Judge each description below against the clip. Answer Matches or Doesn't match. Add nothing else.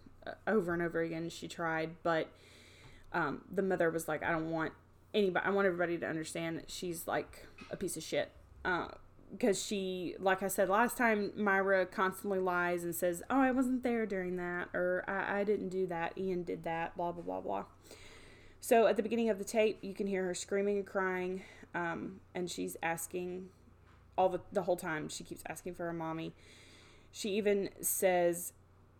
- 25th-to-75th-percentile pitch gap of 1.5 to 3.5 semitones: Matches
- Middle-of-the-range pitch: Matches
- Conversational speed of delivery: Matches